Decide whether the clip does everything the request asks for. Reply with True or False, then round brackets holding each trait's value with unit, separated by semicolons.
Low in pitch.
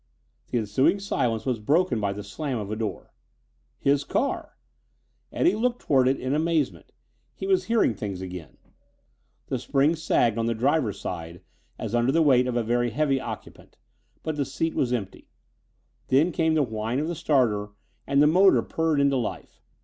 True (130 Hz)